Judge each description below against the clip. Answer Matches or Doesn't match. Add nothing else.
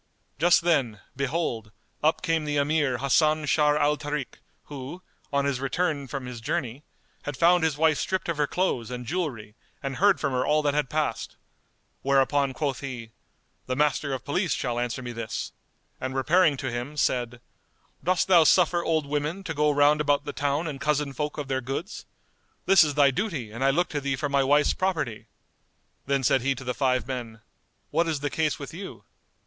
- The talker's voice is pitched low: Doesn't match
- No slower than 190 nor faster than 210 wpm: Matches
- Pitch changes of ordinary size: Matches